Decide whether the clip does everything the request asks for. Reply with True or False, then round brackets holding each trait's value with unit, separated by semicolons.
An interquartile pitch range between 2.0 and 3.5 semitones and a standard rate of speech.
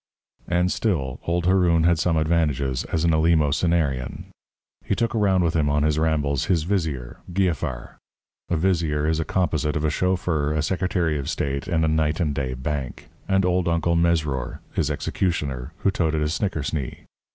True (3.0 semitones; 170 wpm)